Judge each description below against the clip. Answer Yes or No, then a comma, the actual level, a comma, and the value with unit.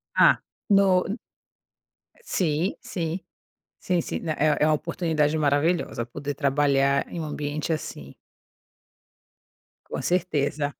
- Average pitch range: Yes, average, 3.1 semitones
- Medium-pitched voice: Yes, medium, 155 Hz